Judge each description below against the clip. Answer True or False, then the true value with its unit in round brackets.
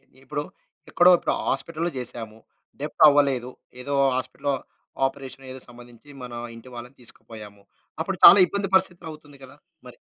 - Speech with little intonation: False (3.7 semitones)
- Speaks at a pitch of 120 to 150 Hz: True (135 Hz)